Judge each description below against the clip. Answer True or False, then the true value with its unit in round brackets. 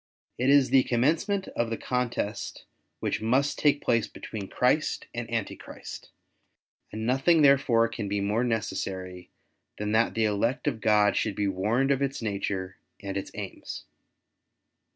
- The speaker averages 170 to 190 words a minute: False (150 wpm)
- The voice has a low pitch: True (115 Hz)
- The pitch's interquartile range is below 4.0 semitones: False (4.3 semitones)